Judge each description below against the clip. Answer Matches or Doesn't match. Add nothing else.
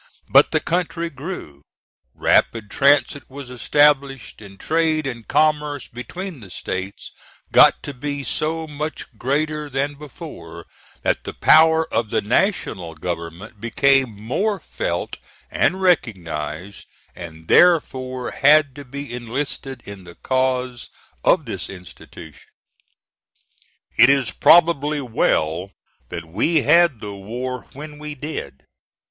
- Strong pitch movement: Matches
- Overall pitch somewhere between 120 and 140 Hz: Matches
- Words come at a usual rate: Doesn't match